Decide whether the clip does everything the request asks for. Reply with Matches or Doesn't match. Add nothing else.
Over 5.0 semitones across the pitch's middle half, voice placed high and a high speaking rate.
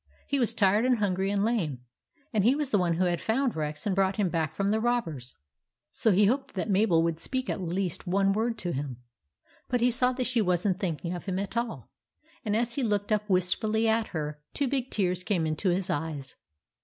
Doesn't match